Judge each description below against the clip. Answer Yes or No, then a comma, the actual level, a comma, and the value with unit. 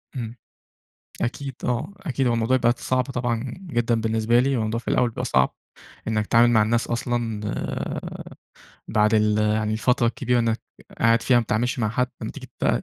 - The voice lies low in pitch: Yes, low, 115 Hz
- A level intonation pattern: Yes, narrow, 1.9 semitones